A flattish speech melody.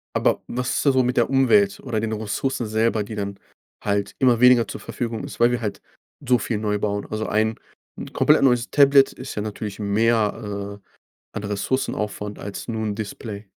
No: average, 3.1 semitones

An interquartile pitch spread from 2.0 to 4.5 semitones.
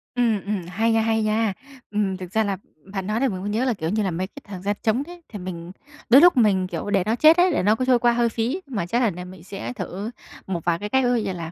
Yes: average, 4.1 semitones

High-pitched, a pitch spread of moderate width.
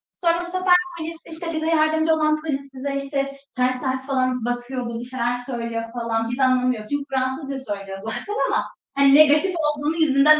Yes: very high, 275 Hz; average, 3.9 semitones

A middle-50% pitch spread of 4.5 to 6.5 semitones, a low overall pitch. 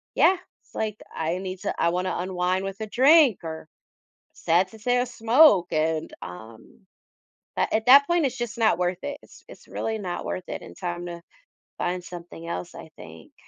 No: wide, 5.4 semitones; medium, 185 Hz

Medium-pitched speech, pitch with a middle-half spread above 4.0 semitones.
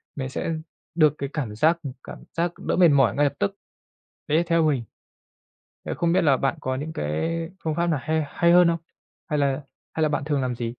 No: medium, 150 Hz; average, 3.6 semitones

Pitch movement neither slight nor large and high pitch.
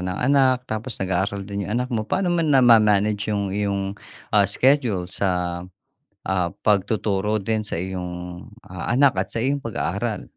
No: average, 3.9 semitones; low, 105 Hz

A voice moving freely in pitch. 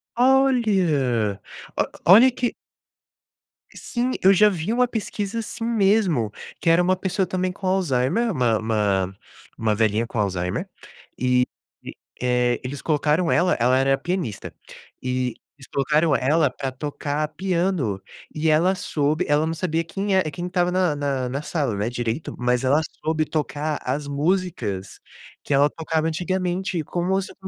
Yes: wide, 6.5 semitones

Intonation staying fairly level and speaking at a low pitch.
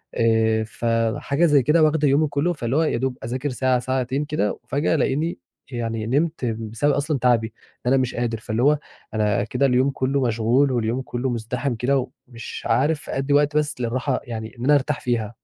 No: average, 3.8 semitones; low, 130 Hz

